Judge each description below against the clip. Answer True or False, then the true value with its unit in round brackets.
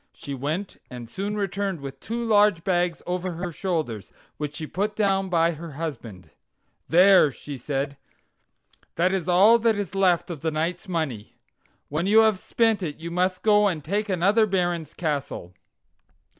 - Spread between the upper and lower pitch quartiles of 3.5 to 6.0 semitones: True (4.6 semitones)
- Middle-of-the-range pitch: True (175 Hz)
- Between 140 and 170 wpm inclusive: True (165 wpm)